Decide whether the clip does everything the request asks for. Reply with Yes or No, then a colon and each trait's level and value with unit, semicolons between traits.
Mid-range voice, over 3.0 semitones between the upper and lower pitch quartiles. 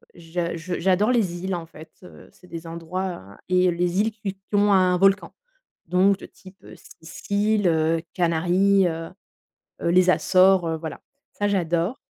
No: medium, 180 Hz; average, 2.7 semitones